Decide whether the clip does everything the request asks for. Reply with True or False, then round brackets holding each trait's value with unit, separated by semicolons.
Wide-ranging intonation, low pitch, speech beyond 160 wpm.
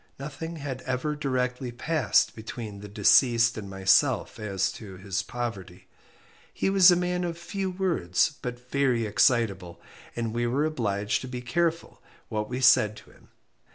False (5.9 semitones; 120 Hz; 155 wpm)